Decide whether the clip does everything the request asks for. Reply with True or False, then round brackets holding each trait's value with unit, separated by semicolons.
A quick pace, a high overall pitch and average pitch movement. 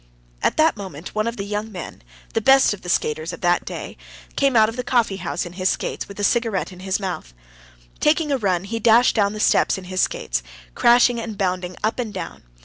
True (230 wpm; 205 Hz; 4.0 semitones)